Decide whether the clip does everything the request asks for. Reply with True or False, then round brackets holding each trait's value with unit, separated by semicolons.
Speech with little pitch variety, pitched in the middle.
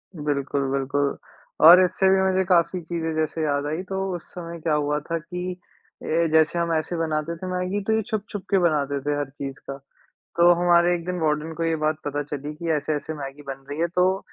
False (3.2 semitones; 160 Hz)